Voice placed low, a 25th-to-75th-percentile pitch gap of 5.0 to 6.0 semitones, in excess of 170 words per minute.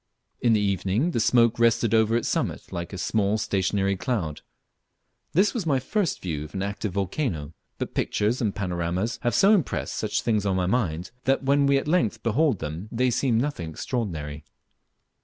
Yes: low, 110 Hz; wide, 5.5 semitones; average, 180 wpm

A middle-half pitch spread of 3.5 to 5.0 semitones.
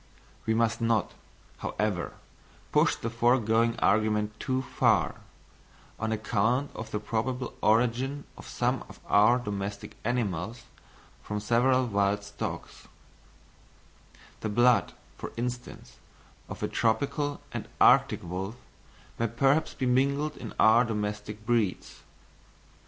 No: average, 2.8 semitones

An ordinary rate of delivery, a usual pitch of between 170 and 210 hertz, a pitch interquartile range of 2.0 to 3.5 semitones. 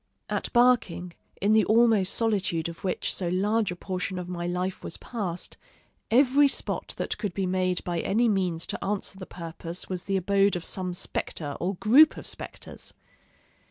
Yes: average, 175 wpm; high, 190 Hz; average, 3.2 semitones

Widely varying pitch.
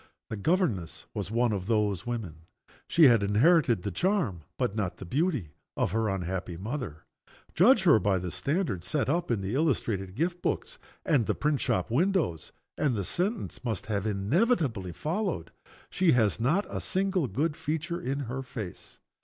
Yes: wide, 8.9 semitones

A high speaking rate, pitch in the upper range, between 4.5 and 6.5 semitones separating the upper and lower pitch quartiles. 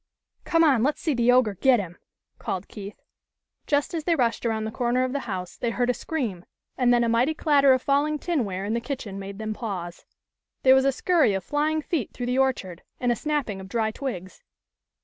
Yes: fast, 220 wpm; high, 245 Hz; average, 5.1 semitones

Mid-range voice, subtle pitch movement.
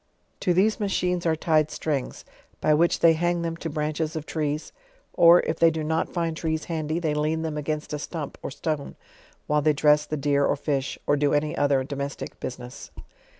Yes: medium, 155 Hz; narrow, 1.9 semitones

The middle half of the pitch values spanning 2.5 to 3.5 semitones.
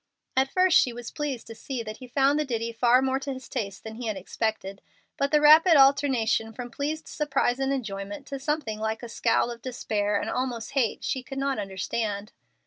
No: average, 3.9 semitones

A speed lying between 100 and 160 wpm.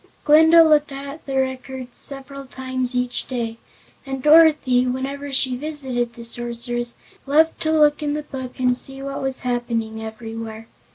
Yes: average, 155 wpm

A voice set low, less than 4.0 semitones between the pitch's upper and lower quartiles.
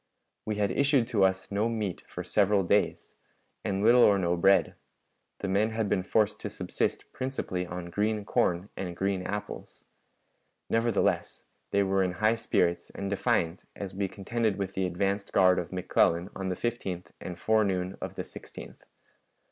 Yes: low, 100 Hz; average, 2.7 semitones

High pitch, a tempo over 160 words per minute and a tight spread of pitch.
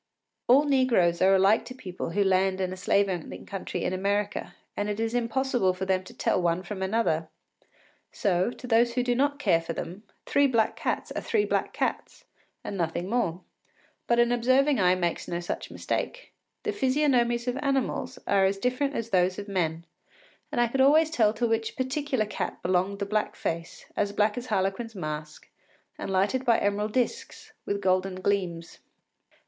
No: high, 205 Hz; average, 185 wpm; average, 5.0 semitones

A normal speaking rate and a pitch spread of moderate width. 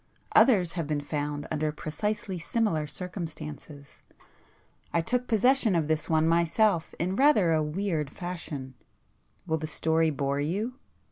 No: slow, 130 wpm; average, 4.6 semitones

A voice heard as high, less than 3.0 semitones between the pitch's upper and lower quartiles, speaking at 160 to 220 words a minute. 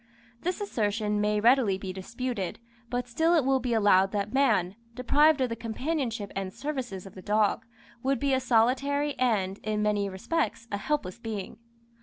No: high, 230 Hz; average, 4.6 semitones; average, 170 wpm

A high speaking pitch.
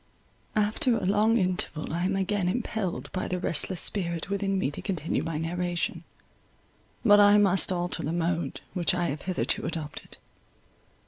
No: medium, 180 Hz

